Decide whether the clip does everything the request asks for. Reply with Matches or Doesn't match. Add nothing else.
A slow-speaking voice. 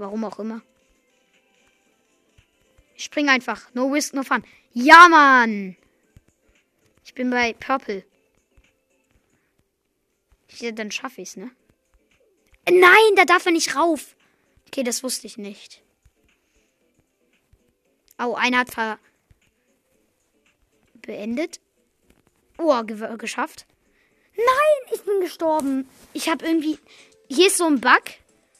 Matches